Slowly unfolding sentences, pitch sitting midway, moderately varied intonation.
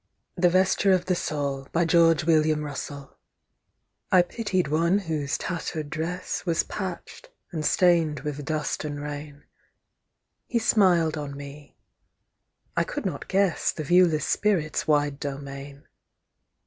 Yes: slow, 115 wpm; medium, 155 Hz; average, 3.8 semitones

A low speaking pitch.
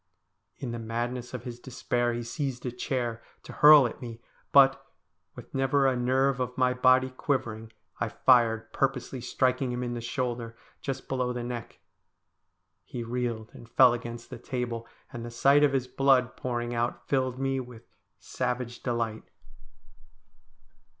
Yes: low, 125 Hz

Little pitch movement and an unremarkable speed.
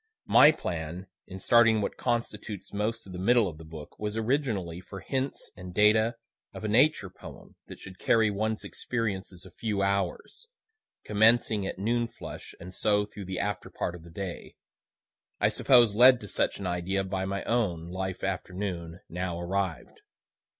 No: average, 3.5 semitones; average, 165 wpm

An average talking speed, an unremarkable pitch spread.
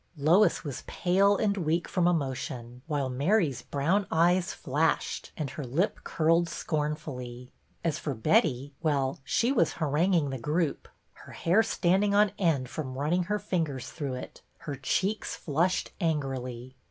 Yes: average, 145 wpm; average, 4.8 semitones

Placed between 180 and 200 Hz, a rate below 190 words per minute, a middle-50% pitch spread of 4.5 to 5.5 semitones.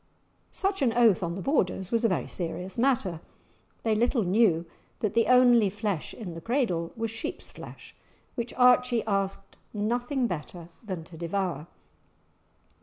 No: high, 215 Hz; average, 150 wpm; average, 5.1 semitones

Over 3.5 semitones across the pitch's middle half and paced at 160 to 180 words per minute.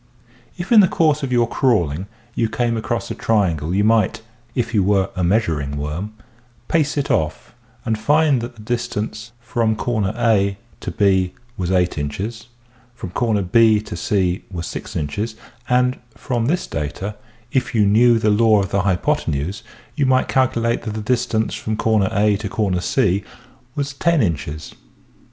Yes: average, 4.1 semitones; average, 165 wpm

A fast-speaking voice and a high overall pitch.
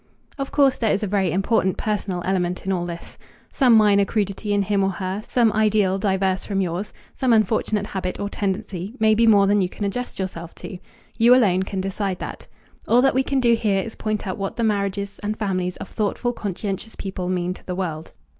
Yes: fast, 210 wpm; high, 200 Hz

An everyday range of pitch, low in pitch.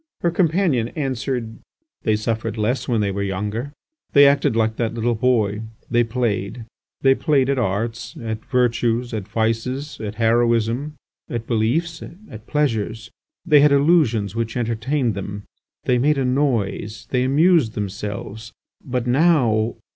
Yes: average, 3.7 semitones; low, 120 Hz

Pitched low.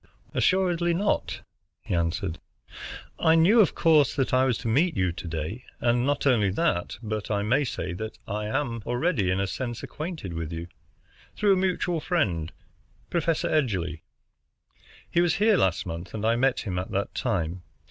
Yes: low, 120 Hz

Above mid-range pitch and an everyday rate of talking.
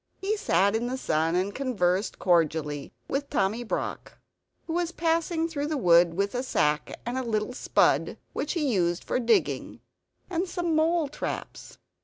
Yes: high, 245 Hz; average, 165 wpm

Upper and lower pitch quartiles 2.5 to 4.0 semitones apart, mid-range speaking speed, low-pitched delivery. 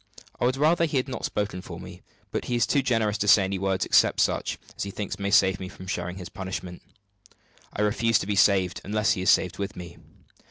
No: average, 3.2 semitones; fast, 230 wpm; low, 100 Hz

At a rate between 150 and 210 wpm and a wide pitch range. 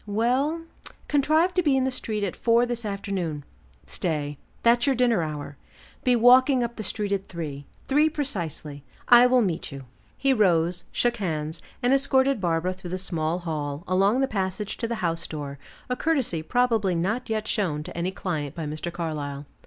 Yes: average, 180 wpm; wide, 7.2 semitones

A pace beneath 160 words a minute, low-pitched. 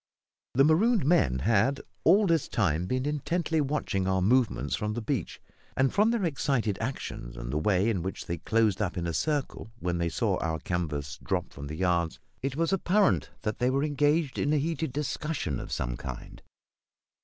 No: average, 190 wpm; low, 115 Hz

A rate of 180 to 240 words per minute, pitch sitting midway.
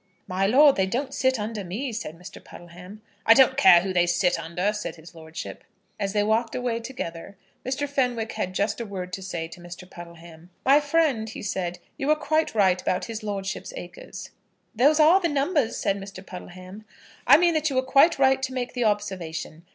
No: average, 200 wpm; high, 210 Hz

